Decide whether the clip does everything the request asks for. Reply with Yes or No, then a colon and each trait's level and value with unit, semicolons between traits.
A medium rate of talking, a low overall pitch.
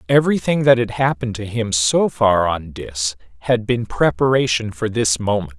Yes: average, 170 wpm; low, 110 Hz